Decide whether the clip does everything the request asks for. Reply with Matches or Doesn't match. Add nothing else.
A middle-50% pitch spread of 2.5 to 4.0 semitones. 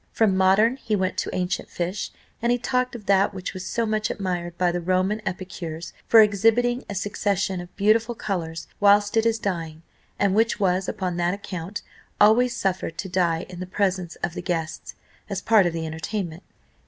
Matches